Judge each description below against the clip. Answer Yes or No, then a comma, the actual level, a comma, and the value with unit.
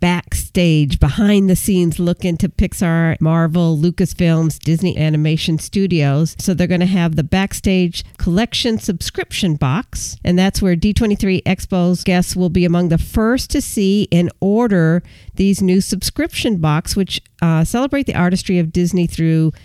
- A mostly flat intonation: No, average, 3.0 semitones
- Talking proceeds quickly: No, average, 150 wpm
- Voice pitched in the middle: Yes, medium, 180 Hz